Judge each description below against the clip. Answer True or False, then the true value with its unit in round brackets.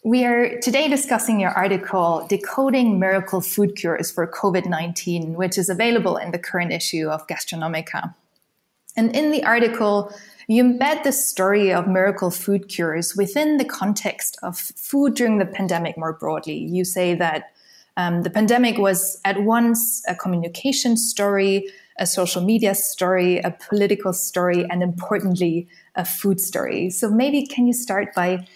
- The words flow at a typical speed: True (155 wpm)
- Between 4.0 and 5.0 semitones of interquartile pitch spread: True (4.3 semitones)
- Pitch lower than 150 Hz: False (195 Hz)